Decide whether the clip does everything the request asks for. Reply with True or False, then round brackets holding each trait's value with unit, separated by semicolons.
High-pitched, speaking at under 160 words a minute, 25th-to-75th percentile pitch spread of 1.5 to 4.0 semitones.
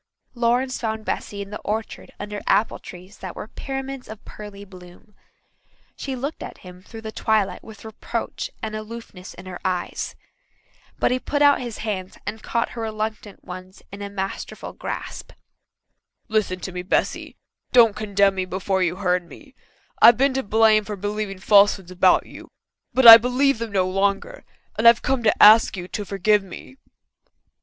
False (210 Hz; 170 wpm; 3.2 semitones)